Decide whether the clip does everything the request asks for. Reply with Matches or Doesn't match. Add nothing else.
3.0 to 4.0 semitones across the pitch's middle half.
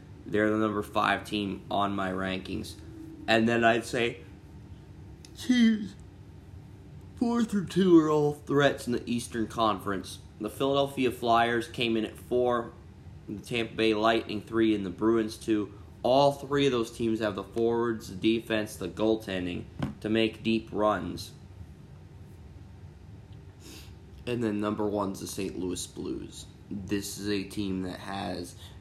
Matches